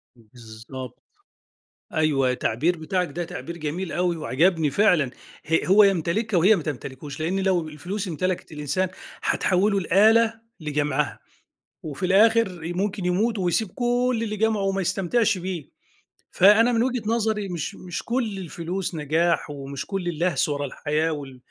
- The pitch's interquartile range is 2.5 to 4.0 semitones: No, average, 4.9 semitones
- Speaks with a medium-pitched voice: Yes, medium, 180 Hz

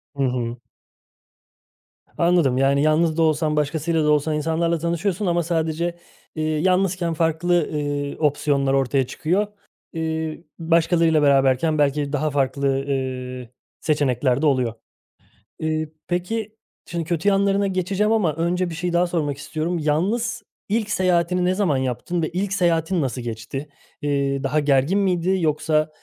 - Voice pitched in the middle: Yes, medium, 160 Hz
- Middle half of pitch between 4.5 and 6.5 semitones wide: No, average, 3.6 semitones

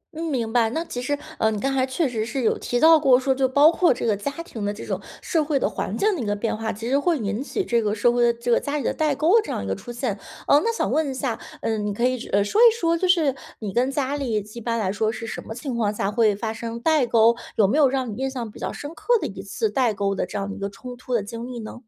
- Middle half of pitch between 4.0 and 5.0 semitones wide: Yes, average, 4.4 semitones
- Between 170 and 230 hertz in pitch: No, high, 245 Hz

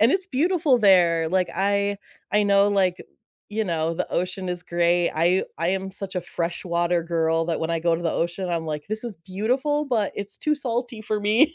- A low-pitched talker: No, high, 190 Hz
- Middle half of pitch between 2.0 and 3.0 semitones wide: No, average, 4.1 semitones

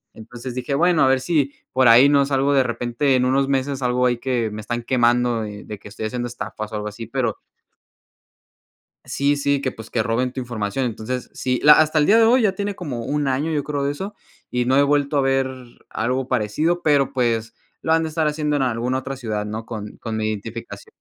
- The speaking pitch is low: Yes, low, 130 Hz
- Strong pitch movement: No, average, 3.5 semitones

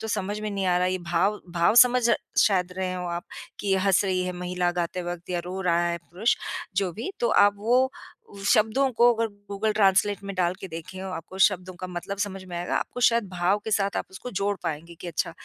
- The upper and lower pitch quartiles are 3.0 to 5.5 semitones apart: No, narrow, 2.6 semitones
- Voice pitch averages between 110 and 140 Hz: No, high, 190 Hz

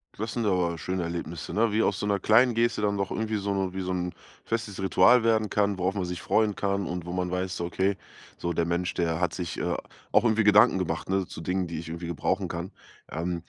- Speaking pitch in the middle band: No, very low, 95 Hz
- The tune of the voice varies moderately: Yes, average, 3.0 semitones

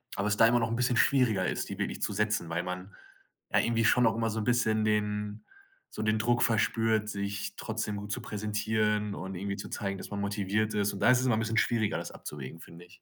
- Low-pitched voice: Yes, low, 105 Hz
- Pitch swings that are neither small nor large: No, narrow, 2.0 semitones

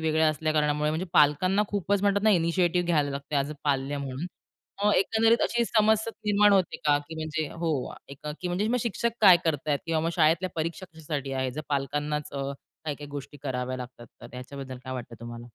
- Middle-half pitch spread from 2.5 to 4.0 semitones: No, average, 4.6 semitones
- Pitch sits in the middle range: Yes, medium, 155 Hz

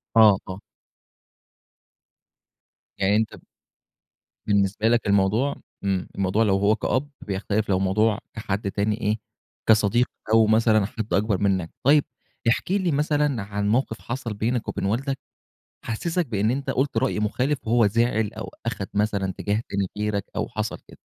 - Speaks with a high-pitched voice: No, low, 110 Hz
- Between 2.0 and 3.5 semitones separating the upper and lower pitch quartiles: Yes, average, 2.9 semitones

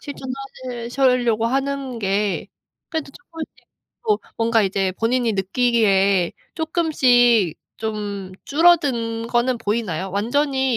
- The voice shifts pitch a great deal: No, average, 4.6 semitones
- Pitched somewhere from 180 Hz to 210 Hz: No, high, 235 Hz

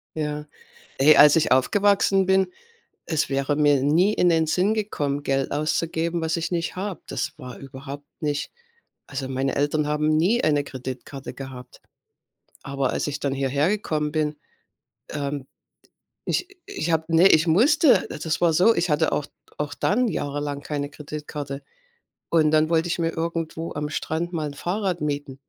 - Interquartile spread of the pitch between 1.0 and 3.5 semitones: Yes, average, 2.9 semitones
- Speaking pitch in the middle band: Yes, medium, 150 Hz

